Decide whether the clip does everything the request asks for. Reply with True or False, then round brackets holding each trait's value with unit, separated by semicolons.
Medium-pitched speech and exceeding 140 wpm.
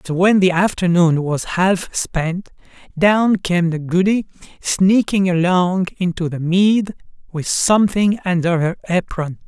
False (180 Hz; 135 wpm)